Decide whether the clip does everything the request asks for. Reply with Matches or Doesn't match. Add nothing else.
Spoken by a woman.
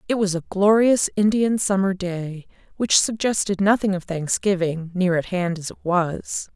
Matches